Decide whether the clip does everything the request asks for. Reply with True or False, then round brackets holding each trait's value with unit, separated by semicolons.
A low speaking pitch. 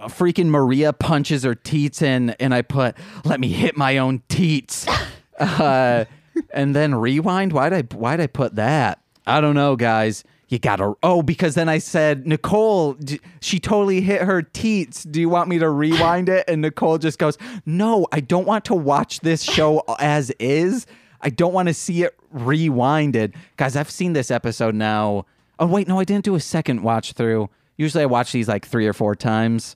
False (150 Hz)